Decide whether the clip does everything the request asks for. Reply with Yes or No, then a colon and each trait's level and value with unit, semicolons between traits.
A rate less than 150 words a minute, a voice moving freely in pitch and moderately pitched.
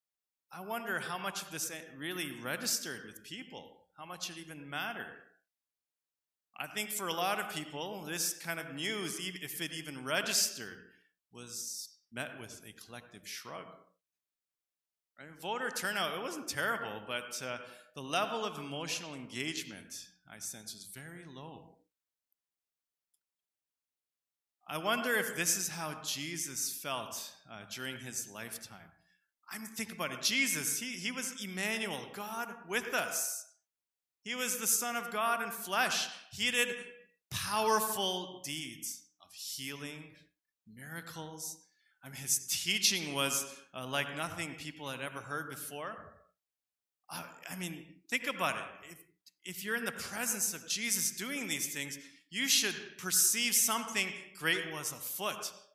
Yes: average, 140 wpm; wide, 6.9 semitones; medium, 165 Hz